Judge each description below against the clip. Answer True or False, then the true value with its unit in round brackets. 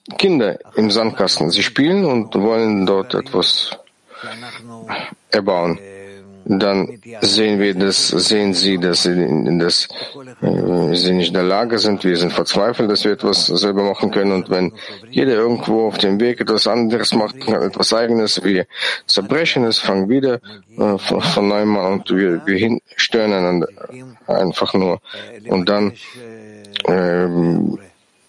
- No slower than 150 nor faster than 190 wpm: False (140 wpm)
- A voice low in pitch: True (100 Hz)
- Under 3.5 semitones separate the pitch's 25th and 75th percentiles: True (3.1 semitones)